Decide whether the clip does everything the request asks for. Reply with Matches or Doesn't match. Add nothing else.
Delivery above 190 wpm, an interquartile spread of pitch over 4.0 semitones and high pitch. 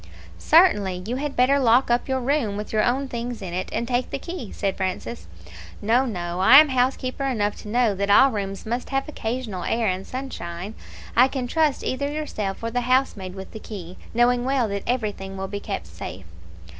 Matches